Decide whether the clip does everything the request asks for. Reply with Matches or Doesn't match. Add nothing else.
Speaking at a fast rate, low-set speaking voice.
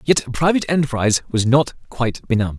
Doesn't match